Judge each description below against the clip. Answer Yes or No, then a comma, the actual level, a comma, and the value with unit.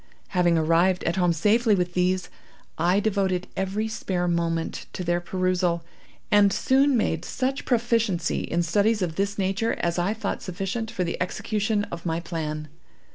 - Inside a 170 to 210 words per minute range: No, average, 160 wpm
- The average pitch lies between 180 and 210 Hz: Yes, medium, 185 Hz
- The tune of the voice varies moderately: Yes, average, 3.3 semitones